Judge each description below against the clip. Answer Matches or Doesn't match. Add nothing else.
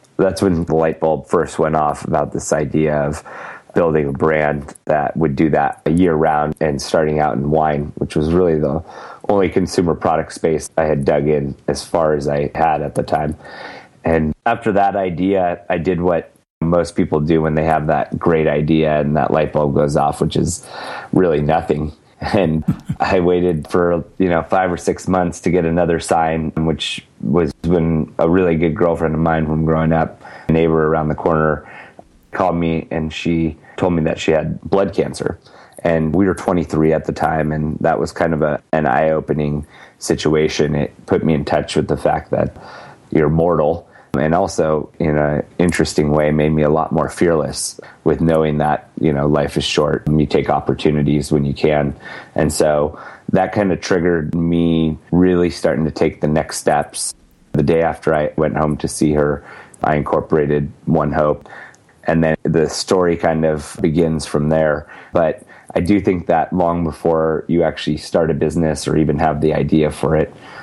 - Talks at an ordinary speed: Matches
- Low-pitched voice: Matches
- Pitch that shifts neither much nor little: Doesn't match